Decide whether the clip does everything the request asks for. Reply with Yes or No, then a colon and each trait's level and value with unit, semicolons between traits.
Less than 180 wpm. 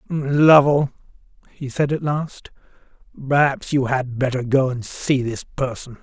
Yes: average, 140 wpm